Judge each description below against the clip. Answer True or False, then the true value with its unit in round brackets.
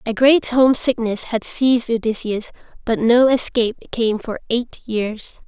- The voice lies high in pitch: True (235 Hz)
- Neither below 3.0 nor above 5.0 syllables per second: True (4.5 syllables/s)